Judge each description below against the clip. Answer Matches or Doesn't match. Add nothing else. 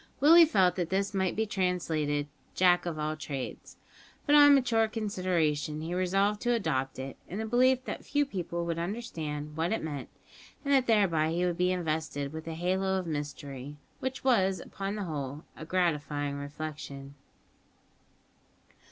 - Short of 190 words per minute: Matches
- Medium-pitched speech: Matches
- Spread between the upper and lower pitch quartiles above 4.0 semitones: Matches